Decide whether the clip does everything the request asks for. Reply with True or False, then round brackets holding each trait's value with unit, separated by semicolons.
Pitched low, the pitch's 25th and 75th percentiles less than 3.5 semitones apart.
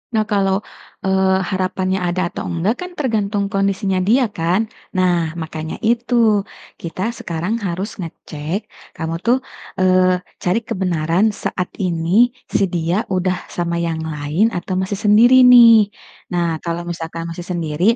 False (185 Hz; 2.9 semitones)